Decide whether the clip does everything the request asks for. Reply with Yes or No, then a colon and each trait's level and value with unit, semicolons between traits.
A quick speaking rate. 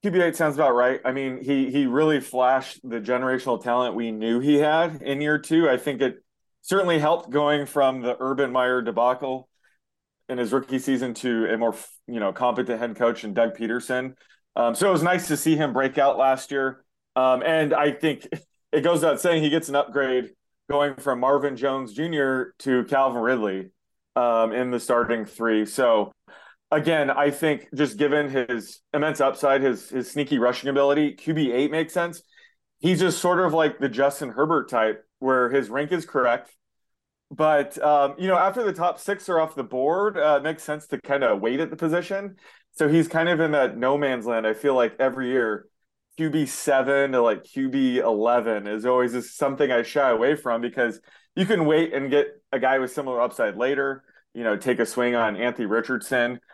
No: average, 195 wpm